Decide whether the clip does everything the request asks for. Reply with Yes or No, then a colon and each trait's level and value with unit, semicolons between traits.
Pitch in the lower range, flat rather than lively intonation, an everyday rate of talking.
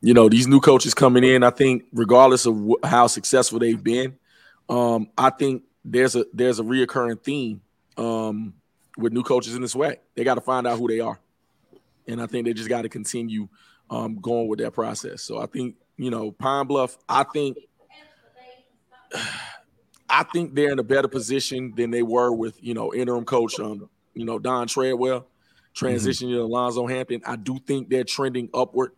Yes: low, 125 Hz; narrow, 1.9 semitones; average, 185 wpm